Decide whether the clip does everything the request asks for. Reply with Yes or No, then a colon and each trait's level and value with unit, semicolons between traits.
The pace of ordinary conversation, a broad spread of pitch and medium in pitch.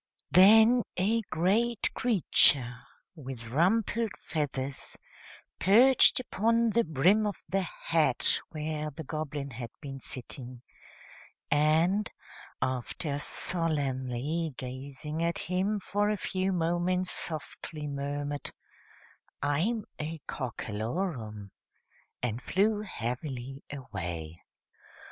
No: slow, 95 wpm; wide, 6.4 semitones; medium, 155 Hz